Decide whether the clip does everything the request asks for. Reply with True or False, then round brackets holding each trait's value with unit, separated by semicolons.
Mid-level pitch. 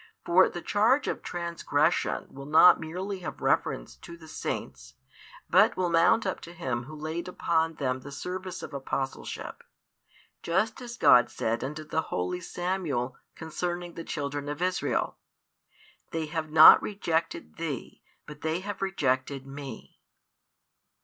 True (160 Hz)